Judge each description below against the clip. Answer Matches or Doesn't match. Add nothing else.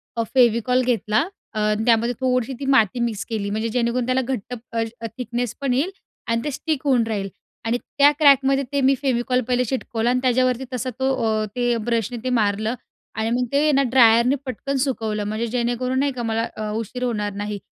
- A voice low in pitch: Doesn't match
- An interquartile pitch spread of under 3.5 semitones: Matches